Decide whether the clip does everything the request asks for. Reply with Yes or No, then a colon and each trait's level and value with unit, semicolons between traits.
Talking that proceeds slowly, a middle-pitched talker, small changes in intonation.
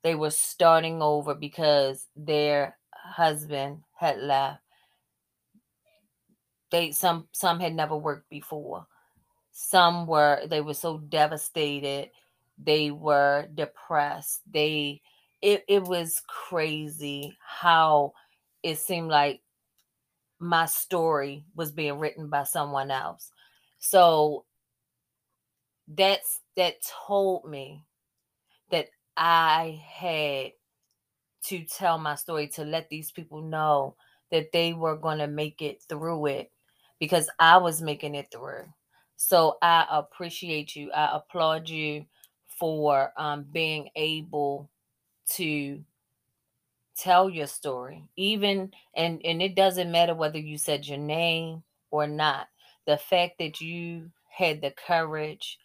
Yes: slow, 115 wpm; medium, 155 Hz; narrow, 2.3 semitones